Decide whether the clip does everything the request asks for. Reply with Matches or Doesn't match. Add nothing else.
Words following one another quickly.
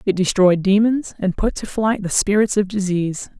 Doesn't match